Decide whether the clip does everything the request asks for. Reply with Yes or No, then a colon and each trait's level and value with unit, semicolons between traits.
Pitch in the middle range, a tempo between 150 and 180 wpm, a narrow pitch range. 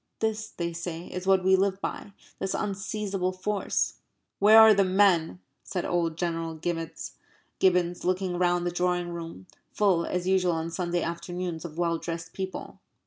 Yes: medium, 180 Hz; average, 155 wpm; narrow, 2.0 semitones